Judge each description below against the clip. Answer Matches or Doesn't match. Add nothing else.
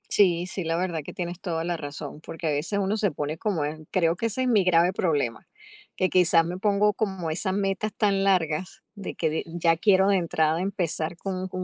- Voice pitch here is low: Doesn't match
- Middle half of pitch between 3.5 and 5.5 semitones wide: Doesn't match